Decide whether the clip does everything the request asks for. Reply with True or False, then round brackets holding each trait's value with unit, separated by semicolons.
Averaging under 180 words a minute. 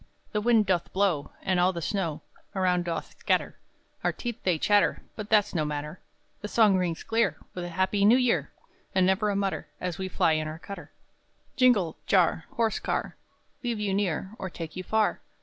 False (200 wpm)